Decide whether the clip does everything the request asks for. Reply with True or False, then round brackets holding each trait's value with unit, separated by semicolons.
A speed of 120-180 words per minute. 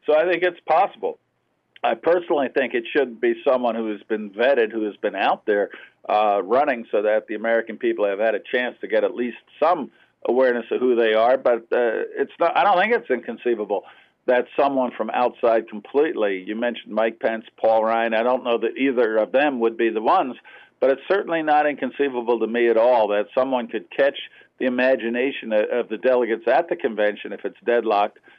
False (205 wpm)